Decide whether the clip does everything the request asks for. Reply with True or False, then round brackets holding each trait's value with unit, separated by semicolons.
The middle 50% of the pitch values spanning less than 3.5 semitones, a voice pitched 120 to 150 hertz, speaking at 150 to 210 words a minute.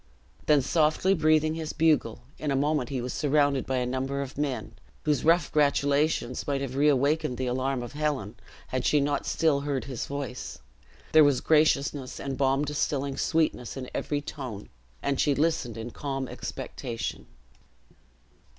True (2.5 semitones; 140 Hz; 160 wpm)